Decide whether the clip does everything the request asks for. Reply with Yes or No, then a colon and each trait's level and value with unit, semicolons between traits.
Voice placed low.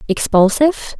No: high, 245 Hz